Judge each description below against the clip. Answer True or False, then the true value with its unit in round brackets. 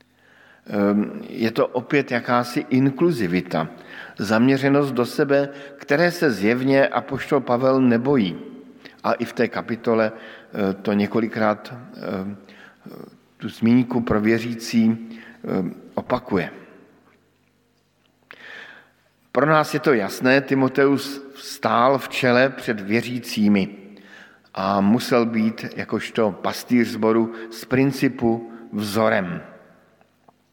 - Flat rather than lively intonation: False (3.6 semitones)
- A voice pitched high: False (120 Hz)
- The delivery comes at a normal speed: False (90 wpm)